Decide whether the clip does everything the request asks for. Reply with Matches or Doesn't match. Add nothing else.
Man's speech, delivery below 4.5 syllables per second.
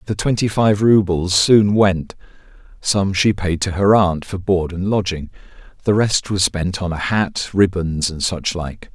Matches